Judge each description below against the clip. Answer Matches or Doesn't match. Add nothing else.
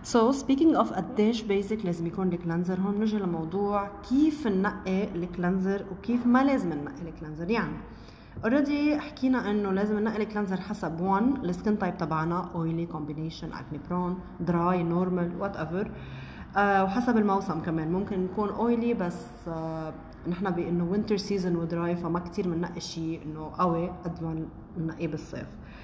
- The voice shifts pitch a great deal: Doesn't match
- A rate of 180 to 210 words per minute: Doesn't match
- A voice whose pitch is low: Doesn't match